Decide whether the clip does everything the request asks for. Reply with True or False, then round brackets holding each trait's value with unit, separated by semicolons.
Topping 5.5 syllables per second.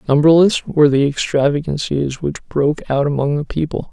False (5.3 syllables/s)